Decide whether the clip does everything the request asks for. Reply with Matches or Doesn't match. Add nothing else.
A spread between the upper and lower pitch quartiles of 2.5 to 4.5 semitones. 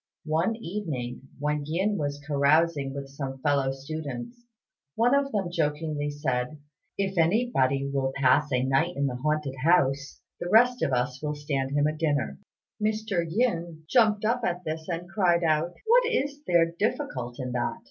Doesn't match